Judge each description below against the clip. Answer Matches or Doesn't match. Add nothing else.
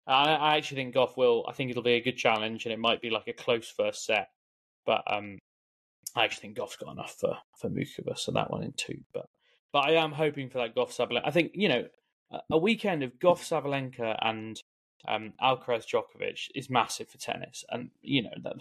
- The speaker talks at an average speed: Doesn't match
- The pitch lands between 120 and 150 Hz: Matches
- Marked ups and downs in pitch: Matches